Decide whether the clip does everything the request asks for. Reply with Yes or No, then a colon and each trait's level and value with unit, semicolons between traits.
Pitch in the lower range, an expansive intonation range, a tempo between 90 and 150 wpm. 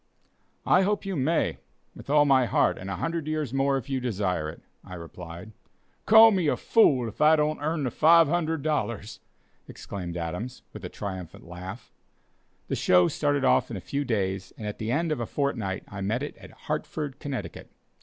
No: low, 130 Hz; wide, 7.8 semitones; average, 185 wpm